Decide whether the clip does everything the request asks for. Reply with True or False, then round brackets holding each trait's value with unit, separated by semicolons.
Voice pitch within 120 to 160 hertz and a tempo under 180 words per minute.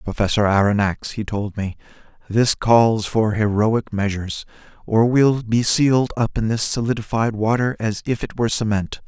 False (110 Hz; 160 wpm)